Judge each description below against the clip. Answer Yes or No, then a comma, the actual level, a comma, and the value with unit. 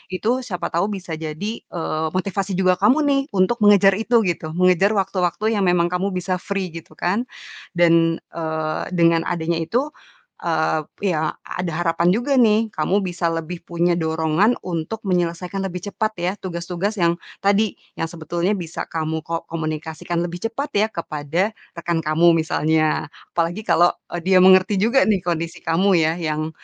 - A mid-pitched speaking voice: Yes, medium, 175 Hz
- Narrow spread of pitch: No, average, 3.0 semitones